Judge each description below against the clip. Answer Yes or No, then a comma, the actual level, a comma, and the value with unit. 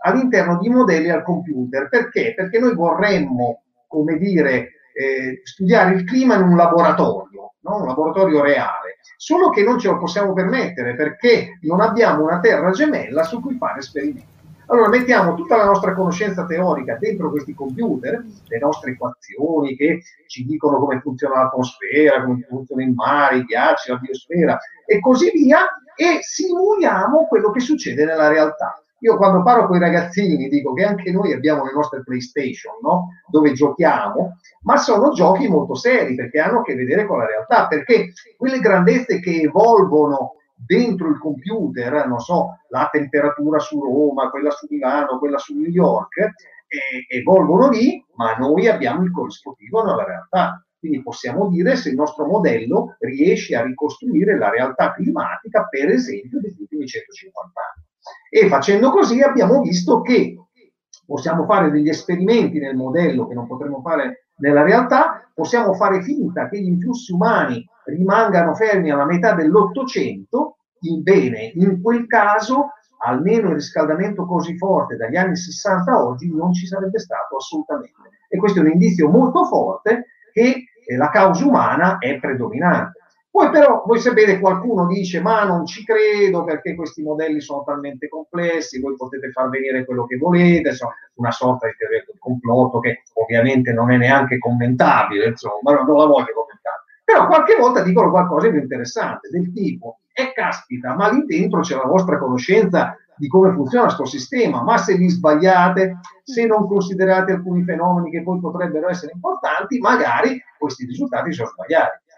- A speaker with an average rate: Yes, average, 160 wpm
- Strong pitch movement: Yes, wide, 7.6 semitones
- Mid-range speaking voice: Yes, medium, 180 Hz